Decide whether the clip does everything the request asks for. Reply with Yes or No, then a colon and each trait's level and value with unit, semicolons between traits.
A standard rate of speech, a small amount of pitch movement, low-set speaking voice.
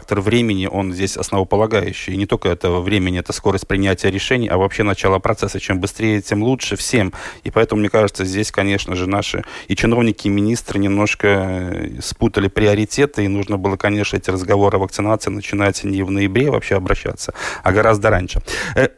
No: fast, 175 wpm; narrow, 1.7 semitones; low, 100 Hz